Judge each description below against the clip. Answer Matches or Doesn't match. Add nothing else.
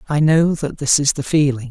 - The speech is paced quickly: Matches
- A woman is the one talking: Doesn't match